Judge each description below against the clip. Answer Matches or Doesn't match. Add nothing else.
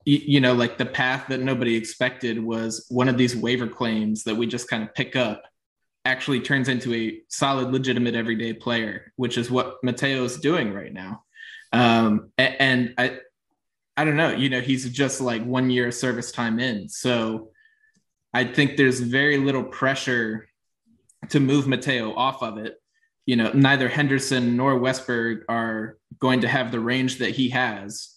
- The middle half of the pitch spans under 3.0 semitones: Matches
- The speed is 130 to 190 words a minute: Matches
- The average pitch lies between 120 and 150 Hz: Matches